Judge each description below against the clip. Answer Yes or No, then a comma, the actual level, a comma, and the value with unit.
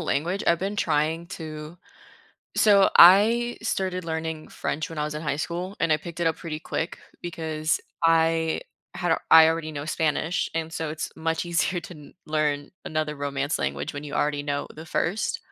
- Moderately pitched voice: Yes, medium, 160 Hz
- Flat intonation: Yes, narrow, 2.0 semitones